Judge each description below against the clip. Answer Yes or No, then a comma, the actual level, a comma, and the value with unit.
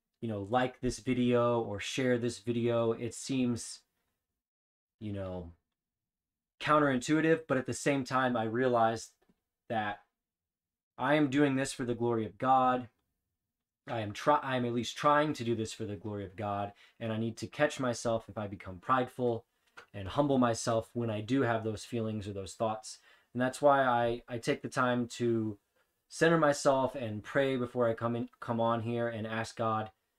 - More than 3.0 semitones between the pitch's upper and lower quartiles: No, average, 2.7 semitones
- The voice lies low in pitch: Yes, low, 120 Hz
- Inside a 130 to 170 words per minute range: No, average, 185 wpm